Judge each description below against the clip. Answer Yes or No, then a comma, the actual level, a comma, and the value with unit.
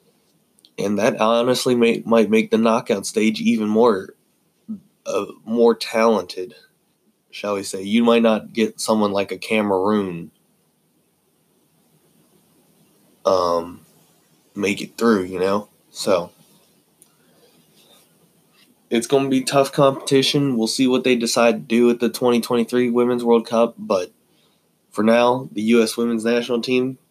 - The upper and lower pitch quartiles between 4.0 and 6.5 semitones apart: No, narrow, 2.5 semitones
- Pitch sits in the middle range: No, low, 115 Hz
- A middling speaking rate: No, slow, 130 wpm